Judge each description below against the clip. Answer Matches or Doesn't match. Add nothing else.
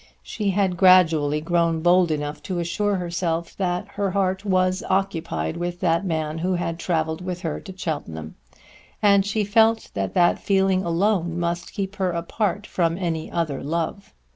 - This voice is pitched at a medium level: Matches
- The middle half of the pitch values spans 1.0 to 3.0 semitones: Matches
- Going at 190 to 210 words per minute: Doesn't match